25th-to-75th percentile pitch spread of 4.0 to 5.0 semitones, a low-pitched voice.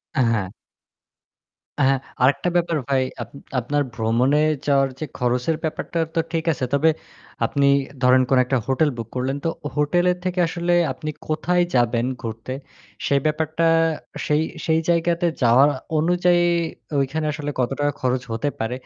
No: average, 4.3 semitones; medium, 145 Hz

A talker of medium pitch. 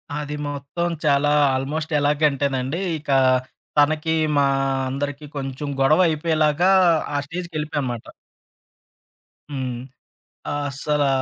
Yes: medium, 145 Hz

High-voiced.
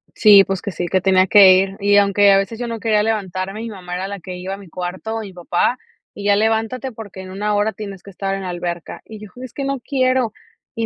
Yes: high, 200 Hz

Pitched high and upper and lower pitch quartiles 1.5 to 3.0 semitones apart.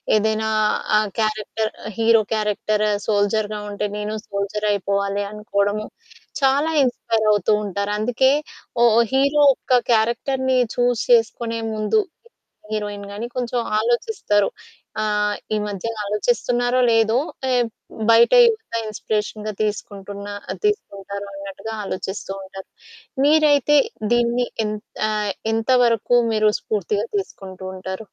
Yes: high, 215 Hz; average, 2.7 semitones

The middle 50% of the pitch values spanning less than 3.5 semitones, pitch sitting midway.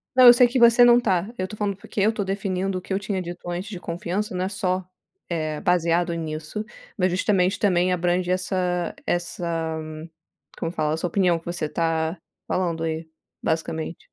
Yes: average, 2.7 semitones; medium, 180 Hz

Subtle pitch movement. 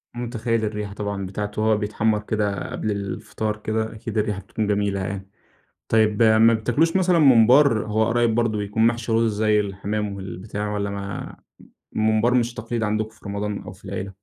Yes: narrow, 1.8 semitones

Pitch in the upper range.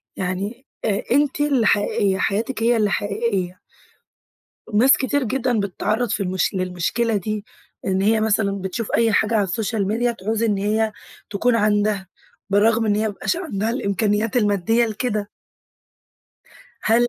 Yes: high, 215 Hz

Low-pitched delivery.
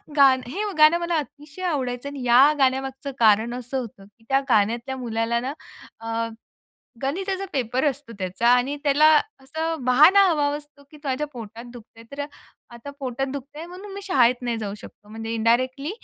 No: very high, 260 Hz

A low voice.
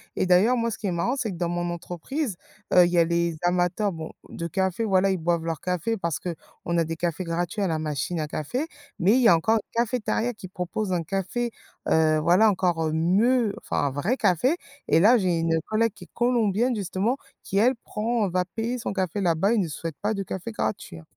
No: medium, 185 Hz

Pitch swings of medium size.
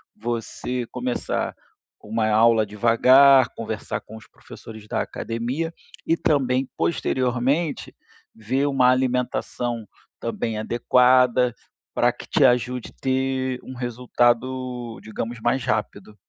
No: narrow, 2.1 semitones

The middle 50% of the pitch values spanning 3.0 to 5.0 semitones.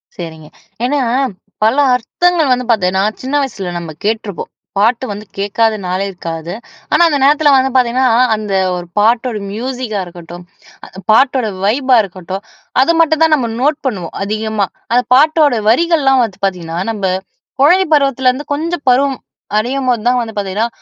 No: wide, 5.6 semitones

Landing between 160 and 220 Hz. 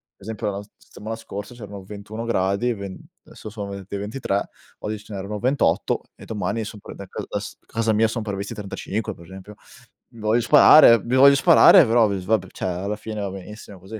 No: low, 105 Hz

